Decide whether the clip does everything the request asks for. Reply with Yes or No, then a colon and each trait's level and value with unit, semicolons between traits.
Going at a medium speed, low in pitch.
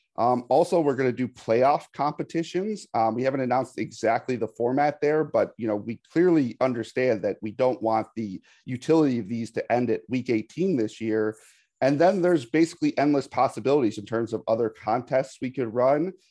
Yes: average, 190 wpm; low, 130 Hz